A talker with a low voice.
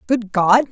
No: high, 220 Hz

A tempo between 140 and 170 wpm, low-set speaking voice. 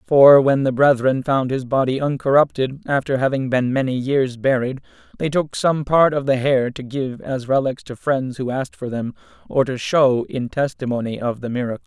No: average, 195 wpm; low, 130 Hz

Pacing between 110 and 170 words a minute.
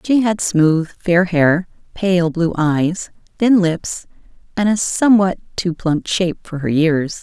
Yes: average, 160 wpm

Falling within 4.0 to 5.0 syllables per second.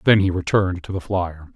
No: 5.8 syllables/s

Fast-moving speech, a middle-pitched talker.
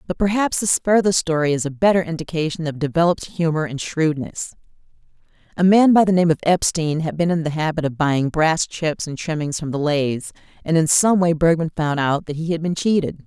Yes: fast, 215 wpm; medium, 165 Hz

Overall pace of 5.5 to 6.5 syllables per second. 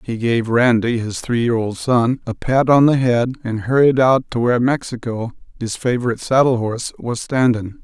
No: 5.0 syllables/s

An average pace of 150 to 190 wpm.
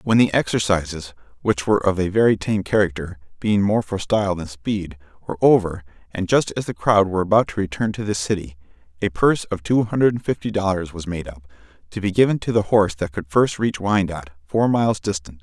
No: average, 200 wpm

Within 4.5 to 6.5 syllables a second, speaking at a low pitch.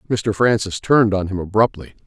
Yes: 5.6 syllables/s; low, 105 Hz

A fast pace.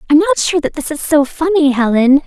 Yes: fast, 240 wpm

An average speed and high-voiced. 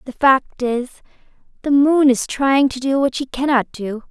Yes: average, 190 wpm; very high, 260 Hz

